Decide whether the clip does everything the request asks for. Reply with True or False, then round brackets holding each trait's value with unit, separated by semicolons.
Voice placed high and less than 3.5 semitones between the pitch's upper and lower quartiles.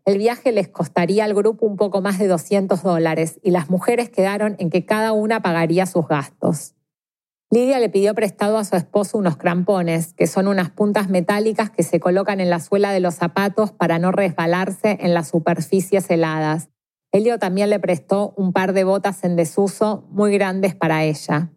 True (195 Hz; 3.1 semitones)